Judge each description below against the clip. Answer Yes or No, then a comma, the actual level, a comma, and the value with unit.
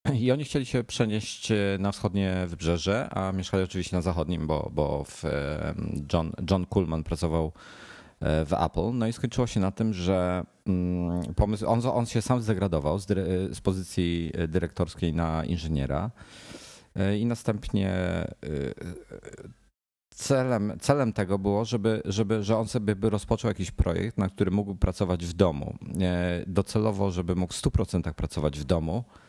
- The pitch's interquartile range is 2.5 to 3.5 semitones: No, average, 3.9 semitones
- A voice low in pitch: Yes, very low, 95 Hz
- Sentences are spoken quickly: No, average, 145 wpm